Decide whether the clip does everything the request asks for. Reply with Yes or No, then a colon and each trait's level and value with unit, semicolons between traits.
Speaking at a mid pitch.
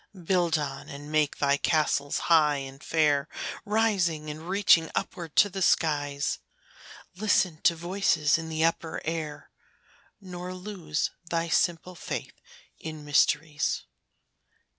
Yes: medium, 160 Hz